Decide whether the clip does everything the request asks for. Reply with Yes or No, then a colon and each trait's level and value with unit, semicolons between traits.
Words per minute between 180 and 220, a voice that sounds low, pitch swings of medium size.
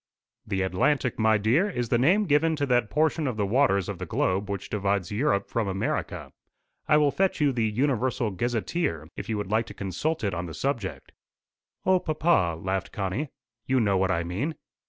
No: average, 195 wpm; low, 115 Hz; wide, 6.8 semitones